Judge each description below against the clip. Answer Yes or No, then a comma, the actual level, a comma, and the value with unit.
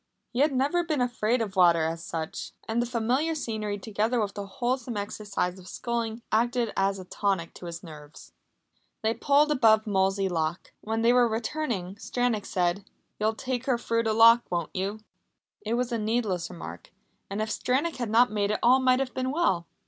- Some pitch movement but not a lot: Yes, average, 4.1 semitones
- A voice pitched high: Yes, high, 220 Hz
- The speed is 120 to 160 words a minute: No, average, 190 wpm